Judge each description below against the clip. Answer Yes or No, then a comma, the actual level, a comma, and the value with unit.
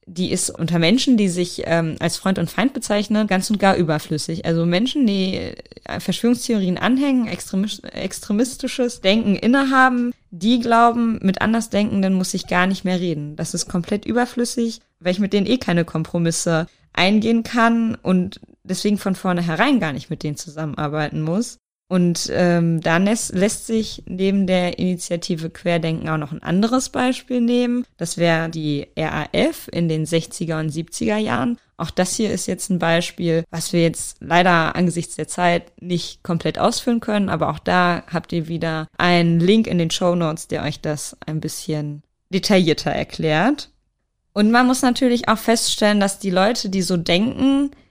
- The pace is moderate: Yes, average, 165 wpm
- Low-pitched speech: No, medium, 185 Hz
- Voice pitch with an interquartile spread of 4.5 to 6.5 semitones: Yes, average, 5.1 semitones